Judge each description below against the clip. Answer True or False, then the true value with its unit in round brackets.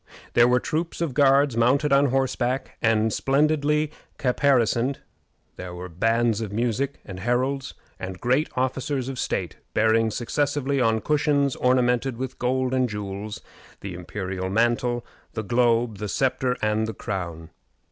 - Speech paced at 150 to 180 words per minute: False (140 wpm)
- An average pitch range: True (3.6 semitones)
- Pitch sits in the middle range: False (120 Hz)